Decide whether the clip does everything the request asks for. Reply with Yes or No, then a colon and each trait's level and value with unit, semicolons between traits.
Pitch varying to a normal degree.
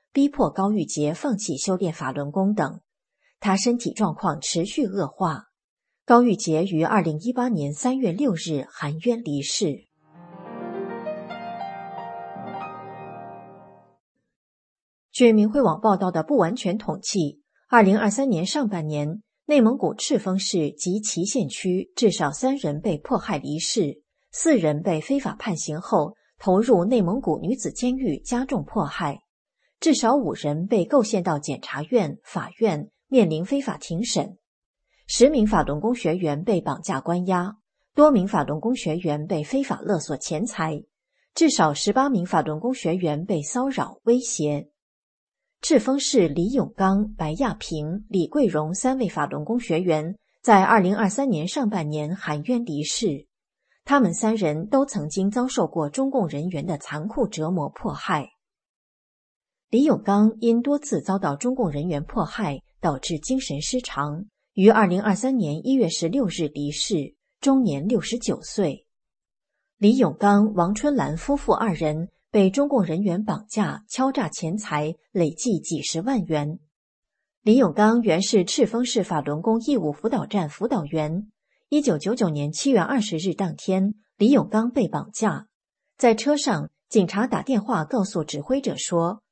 No: wide, 7.2 semitones